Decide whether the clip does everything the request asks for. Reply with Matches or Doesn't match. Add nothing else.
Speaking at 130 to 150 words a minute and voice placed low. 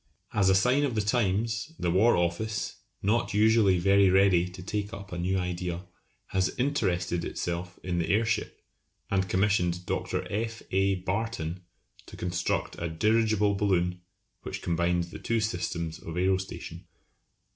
Matches